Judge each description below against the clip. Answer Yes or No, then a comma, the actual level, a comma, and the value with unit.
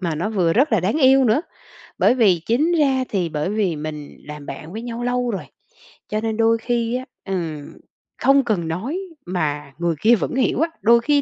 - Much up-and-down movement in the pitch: Yes, wide, 6.5 semitones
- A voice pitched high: Yes, high, 220 Hz